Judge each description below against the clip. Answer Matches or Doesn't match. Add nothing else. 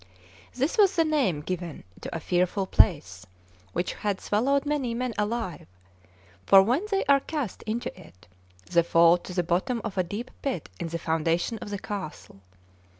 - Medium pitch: Doesn't match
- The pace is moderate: Matches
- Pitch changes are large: Matches